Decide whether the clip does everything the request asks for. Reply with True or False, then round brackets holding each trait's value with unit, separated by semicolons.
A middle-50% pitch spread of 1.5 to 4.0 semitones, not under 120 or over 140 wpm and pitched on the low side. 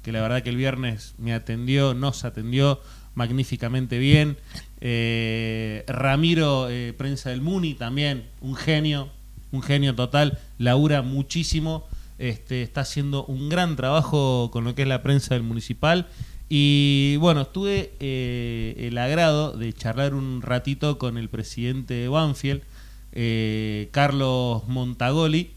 True (2.9 semitones; 135 wpm; 130 Hz)